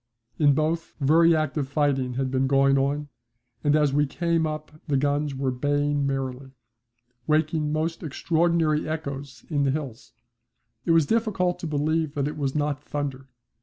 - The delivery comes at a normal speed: Yes, average, 165 wpm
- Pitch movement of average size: No, narrow, 2.3 semitones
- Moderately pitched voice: Yes, medium, 145 Hz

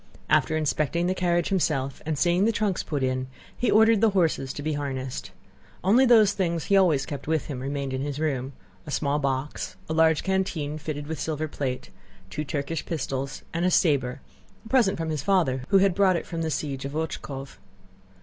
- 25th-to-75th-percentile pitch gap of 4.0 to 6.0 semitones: Yes, average, 4.7 semitones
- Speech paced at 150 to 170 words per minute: No, average, 195 wpm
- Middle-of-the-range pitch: Yes, medium, 155 Hz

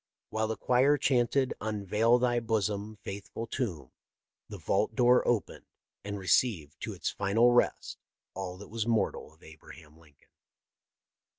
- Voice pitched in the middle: No, low, 110 Hz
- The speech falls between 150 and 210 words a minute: No, average, 140 wpm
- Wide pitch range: No, average, 4.4 semitones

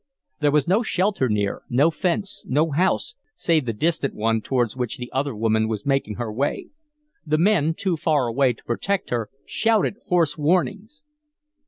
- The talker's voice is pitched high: No, medium, 145 Hz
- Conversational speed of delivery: Yes, average, 170 wpm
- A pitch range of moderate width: No, wide, 6.9 semitones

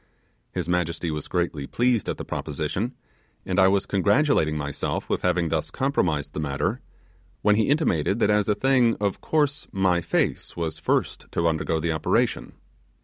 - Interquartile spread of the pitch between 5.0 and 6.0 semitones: Yes, wide, 5.5 semitones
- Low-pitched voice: Yes, very low, 90 Hz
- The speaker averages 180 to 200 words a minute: No, average, 165 wpm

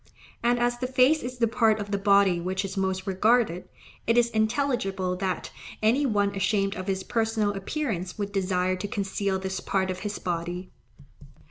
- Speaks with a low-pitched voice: No, high, 200 Hz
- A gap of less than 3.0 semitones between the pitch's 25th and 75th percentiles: No, average, 3.5 semitones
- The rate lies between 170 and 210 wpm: Yes, average, 175 wpm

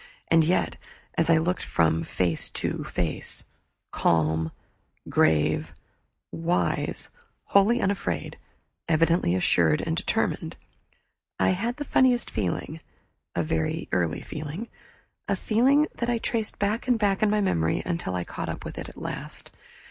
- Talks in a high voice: No, medium, 165 Hz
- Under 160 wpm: Yes, slow, 135 wpm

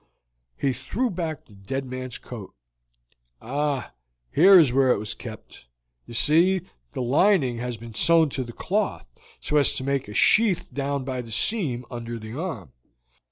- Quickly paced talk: No, average, 165 wpm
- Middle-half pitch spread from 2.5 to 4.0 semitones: No, average, 4.9 semitones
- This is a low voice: Yes, low, 130 Hz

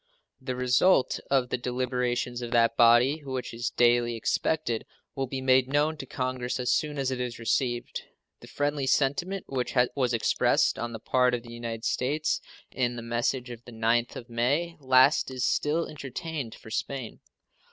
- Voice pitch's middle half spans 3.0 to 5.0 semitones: No, narrow, 2.4 semitones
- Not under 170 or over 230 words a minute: Yes, average, 175 wpm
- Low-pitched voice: Yes, low, 125 Hz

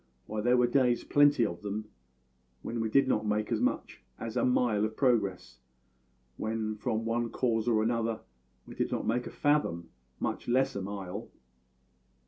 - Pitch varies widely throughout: No, narrow, 2.4 semitones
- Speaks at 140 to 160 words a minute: No, average, 170 wpm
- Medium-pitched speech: No, low, 115 Hz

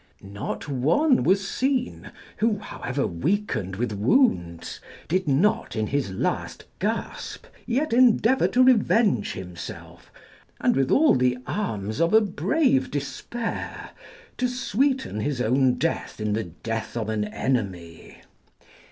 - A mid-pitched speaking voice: Yes, medium, 145 Hz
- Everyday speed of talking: No, slow, 125 wpm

